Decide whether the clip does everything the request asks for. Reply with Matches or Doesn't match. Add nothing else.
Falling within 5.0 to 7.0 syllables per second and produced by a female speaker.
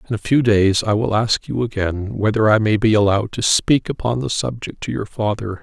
Doesn't match